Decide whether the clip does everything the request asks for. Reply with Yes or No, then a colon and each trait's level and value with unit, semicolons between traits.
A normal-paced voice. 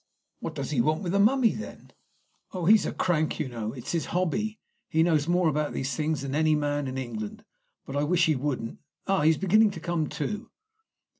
No: fast, 210 wpm